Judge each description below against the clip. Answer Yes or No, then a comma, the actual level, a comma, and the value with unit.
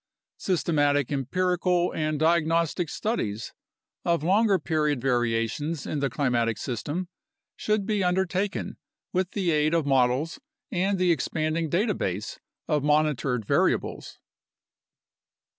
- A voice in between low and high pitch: Yes, medium, 155 Hz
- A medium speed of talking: No, slow, 115 wpm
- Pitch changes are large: No, average, 4.5 semitones